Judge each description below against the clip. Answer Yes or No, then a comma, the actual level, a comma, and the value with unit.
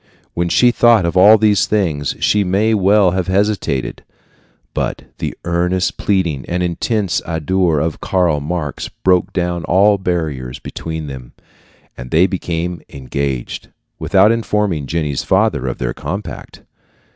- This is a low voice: Yes, very low, 90 Hz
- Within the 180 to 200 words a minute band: No, slow, 135 wpm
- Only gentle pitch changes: No, average, 4.2 semitones